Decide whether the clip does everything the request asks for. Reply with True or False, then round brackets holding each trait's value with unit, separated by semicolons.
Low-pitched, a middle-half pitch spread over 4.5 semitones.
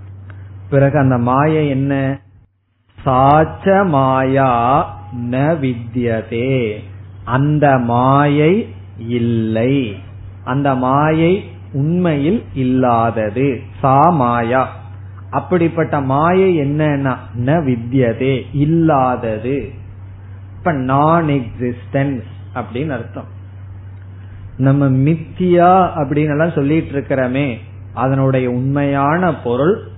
True (130 Hz; 5.0 semitones)